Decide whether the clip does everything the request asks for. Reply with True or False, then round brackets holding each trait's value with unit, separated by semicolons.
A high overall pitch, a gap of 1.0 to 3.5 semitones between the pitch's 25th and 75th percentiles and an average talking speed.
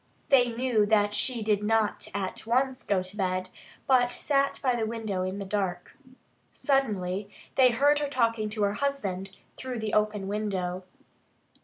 False (215 Hz; 4.1 semitones; 160 wpm)